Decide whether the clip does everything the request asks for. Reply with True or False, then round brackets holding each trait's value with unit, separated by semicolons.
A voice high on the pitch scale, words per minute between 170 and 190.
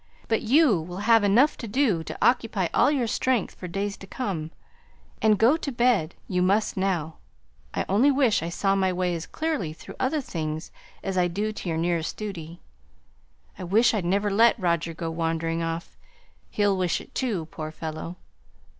True (195 Hz; 180 wpm)